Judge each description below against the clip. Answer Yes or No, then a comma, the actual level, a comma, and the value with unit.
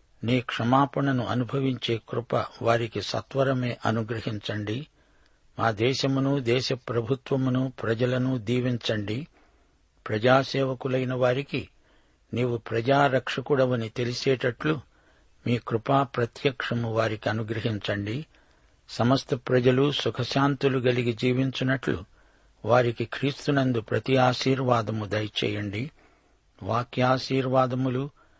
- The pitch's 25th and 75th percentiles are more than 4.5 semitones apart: No, average, 2.7 semitones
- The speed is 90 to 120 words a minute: No, slow, 70 wpm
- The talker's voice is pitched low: Yes, low, 125 Hz